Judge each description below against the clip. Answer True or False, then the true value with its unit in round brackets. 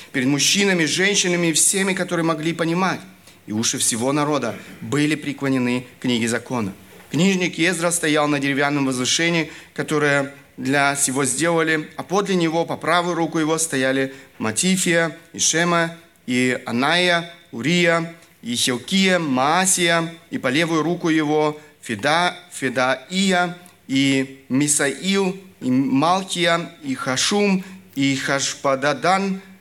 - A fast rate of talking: False (120 wpm)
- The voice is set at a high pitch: False (160 Hz)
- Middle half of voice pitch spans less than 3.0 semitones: False (4.3 semitones)